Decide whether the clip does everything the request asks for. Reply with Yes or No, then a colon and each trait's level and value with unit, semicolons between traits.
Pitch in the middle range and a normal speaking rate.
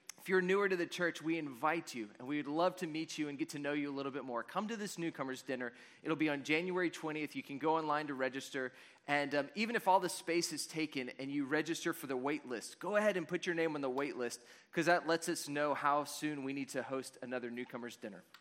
No: medium, 150 Hz; fast, 265 wpm